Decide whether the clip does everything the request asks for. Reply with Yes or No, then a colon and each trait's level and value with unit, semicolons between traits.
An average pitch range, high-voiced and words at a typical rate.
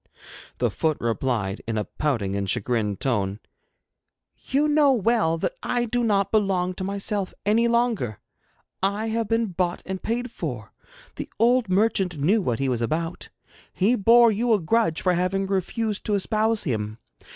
No: wide, 8.7 semitones; high, 195 Hz; average, 160 wpm